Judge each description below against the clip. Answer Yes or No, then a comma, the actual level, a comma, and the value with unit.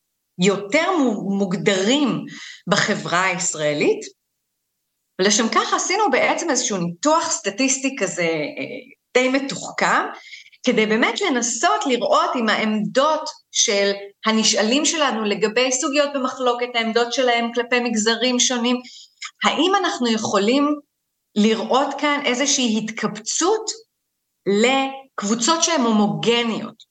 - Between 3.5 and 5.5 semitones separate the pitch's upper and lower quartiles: Yes, average, 5.2 semitones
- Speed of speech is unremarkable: No, slow, 90 wpm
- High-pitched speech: Yes, high, 245 Hz